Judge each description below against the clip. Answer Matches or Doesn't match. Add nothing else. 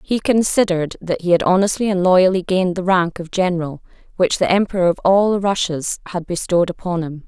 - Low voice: Doesn't match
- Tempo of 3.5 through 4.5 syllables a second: Doesn't match